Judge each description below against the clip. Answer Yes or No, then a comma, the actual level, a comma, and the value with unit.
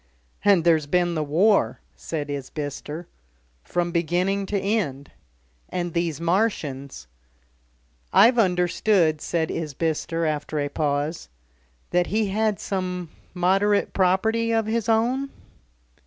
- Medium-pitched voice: Yes, medium, 175 Hz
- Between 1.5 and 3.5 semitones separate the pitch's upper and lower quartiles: No, average, 4.7 semitones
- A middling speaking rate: No, slow, 110 wpm